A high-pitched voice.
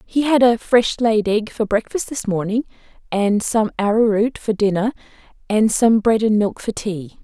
Yes: high, 220 Hz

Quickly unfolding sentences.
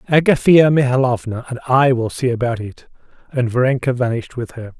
No: average, 165 wpm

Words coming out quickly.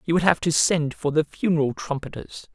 Yes: fast, 210 wpm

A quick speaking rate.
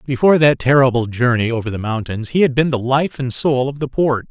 Yes: fast, 235 wpm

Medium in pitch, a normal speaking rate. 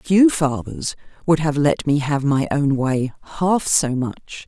Yes: medium, 145 Hz; average, 175 wpm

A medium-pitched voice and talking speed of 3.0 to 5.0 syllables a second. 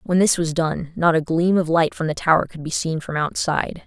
No: medium, 165 Hz; 5.4 syllables/s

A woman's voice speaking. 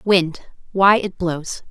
Yes: female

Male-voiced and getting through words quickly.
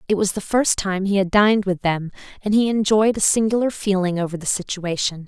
No: female; fast, 215 wpm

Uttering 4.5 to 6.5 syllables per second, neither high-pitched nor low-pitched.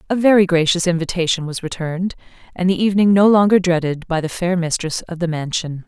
Yes: 6.1 syllables/s; medium, 175 Hz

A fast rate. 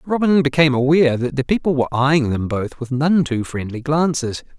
No: average, 195 wpm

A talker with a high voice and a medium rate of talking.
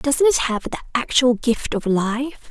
Yes: very high, 250 Hz; average, 190 wpm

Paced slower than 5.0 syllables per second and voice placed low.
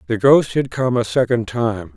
Yes: 4.5 syllables/s; low, 120 Hz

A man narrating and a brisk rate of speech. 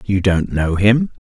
No: male; average, 190 wpm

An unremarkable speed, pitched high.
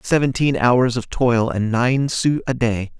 No: average, 180 wpm; low, 120 Hz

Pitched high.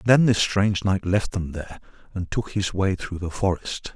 No: very low, 95 Hz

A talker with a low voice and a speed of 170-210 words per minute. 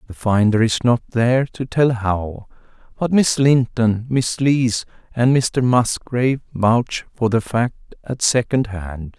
No: low, 120 Hz; average, 150 wpm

